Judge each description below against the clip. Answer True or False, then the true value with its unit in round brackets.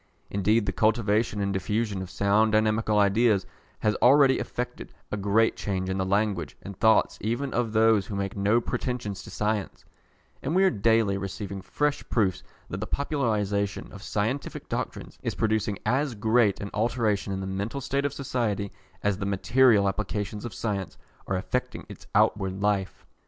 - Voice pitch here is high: False (105 Hz)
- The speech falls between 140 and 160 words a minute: False (170 wpm)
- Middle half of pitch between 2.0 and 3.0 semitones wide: True (2.5 semitones)